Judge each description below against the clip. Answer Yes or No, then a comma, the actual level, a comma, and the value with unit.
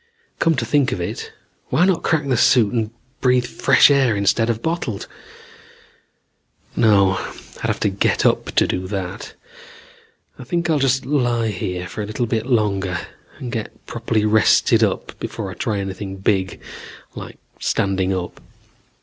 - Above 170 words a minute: No, average, 155 wpm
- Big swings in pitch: No, average, 4.7 semitones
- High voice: No, low, 110 Hz